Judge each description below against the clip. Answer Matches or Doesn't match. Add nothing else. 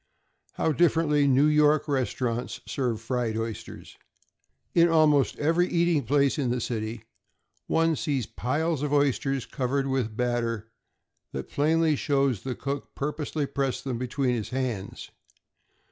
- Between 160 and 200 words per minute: Doesn't match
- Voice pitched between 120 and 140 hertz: Matches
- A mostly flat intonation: Doesn't match